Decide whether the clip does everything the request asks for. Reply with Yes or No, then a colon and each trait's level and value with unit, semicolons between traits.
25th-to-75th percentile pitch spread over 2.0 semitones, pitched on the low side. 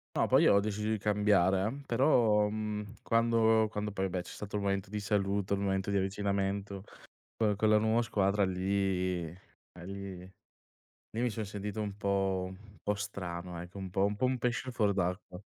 No: narrow, 1.7 semitones; low, 100 Hz